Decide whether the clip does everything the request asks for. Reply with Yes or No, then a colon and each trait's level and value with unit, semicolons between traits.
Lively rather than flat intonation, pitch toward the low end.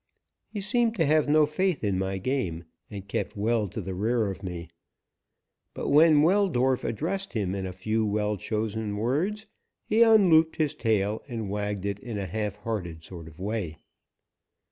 Yes: wide, 7.6 semitones; low, 110 Hz